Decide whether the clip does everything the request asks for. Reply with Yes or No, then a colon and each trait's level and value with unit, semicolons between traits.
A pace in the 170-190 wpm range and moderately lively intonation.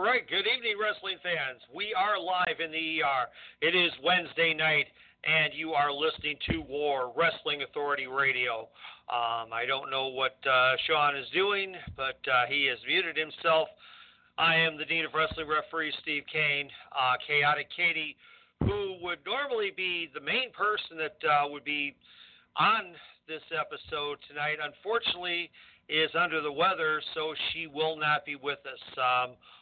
No: average, 160 wpm; average, 3.5 semitones